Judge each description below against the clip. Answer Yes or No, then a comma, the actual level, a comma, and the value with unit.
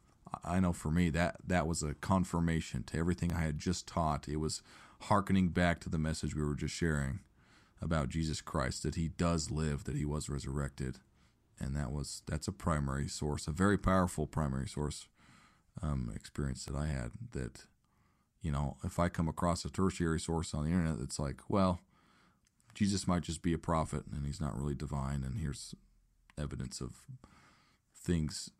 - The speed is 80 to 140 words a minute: No, average, 180 wpm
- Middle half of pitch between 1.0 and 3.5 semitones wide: Yes, average, 3.2 semitones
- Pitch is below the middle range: Yes, very low, 80 Hz